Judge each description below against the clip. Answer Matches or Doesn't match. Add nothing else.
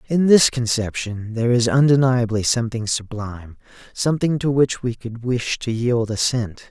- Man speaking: Matches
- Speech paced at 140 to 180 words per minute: Matches